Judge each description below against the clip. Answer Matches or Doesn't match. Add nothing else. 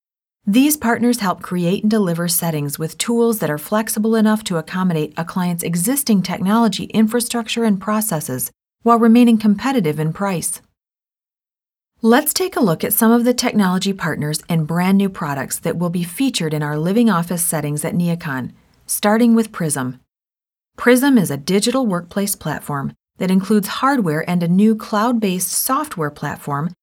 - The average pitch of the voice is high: Matches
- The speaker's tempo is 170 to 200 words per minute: Doesn't match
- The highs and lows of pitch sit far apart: Matches